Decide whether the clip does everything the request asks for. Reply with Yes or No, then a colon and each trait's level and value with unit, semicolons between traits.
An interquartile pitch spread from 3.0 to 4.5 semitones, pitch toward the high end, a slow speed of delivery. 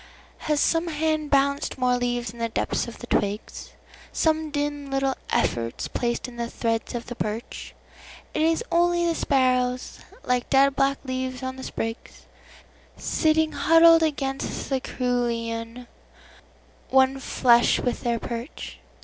Yes: average, 3.6 semitones; very high, 260 Hz; slow, 130 wpm